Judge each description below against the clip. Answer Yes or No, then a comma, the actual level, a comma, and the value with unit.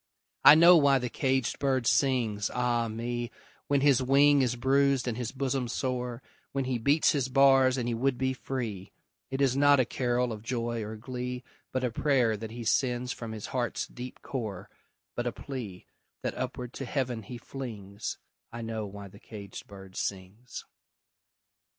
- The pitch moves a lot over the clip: No, average, 2.8 semitones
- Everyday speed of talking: Yes, average, 175 wpm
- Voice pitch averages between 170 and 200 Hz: No, low, 125 Hz